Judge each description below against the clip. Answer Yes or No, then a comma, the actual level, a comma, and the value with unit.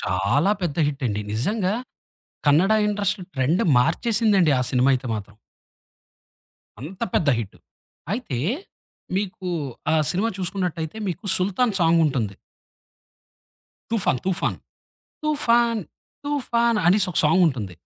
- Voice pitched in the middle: Yes, medium, 180 Hz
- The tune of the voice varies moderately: No, wide, 7.2 semitones